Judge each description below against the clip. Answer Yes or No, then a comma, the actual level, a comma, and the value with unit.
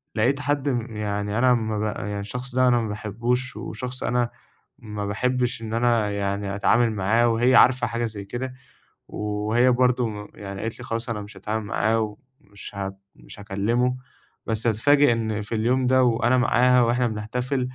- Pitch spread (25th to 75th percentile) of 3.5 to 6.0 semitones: No, average, 3.0 semitones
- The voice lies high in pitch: No, low, 115 Hz